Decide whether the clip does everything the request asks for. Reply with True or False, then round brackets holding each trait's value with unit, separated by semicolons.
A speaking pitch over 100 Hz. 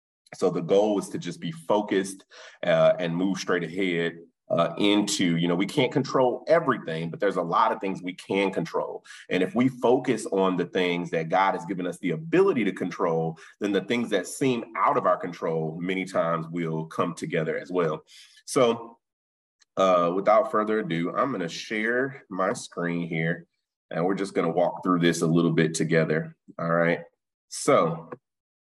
False (85 Hz)